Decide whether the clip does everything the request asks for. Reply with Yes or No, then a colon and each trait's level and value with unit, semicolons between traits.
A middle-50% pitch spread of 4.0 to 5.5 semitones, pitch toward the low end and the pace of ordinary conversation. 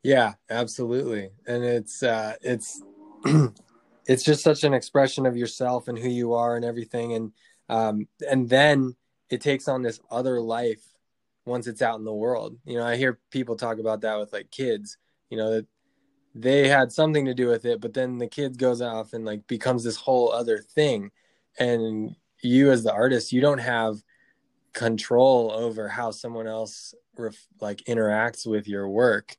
No: average, 2.9 semitones; low, 120 Hz; average, 180 wpm